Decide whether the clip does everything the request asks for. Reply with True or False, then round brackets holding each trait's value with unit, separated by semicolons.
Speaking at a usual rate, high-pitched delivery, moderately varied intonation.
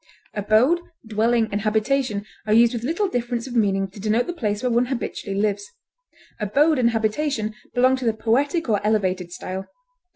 True (170 wpm; 225 Hz; 3.4 semitones)